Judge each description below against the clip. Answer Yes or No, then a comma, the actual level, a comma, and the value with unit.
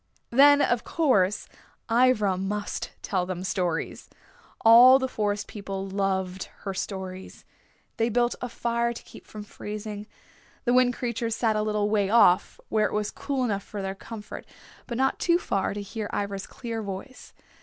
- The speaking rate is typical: Yes, average, 165 wpm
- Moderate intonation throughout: Yes, average, 3.4 semitones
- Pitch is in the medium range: No, high, 210 Hz